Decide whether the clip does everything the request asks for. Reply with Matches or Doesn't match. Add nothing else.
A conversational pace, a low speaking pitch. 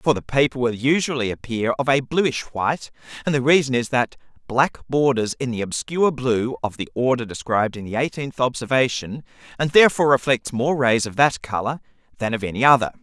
Matches